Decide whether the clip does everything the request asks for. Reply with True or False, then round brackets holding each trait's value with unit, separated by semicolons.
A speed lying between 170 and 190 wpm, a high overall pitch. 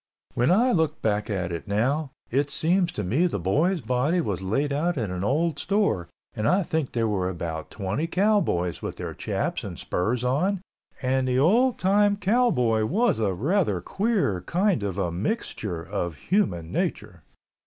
False (175 wpm; 130 Hz)